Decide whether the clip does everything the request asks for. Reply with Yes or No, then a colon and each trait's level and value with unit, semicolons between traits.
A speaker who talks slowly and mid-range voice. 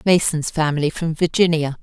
Yes: slow, 130 wpm; medium, 160 Hz